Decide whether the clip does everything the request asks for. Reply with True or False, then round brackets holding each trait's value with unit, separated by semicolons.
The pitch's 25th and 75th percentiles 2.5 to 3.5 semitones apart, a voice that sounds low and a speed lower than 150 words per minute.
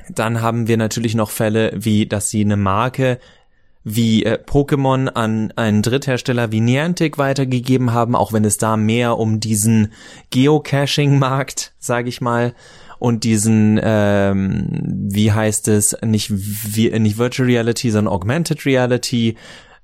True (2.8 semitones; 115 Hz; 140 wpm)